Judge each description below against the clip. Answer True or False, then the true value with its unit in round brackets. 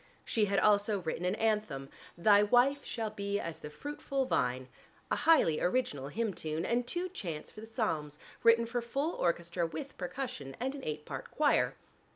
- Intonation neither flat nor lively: False (7.0 semitones)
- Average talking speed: True (180 wpm)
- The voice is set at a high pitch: True (210 Hz)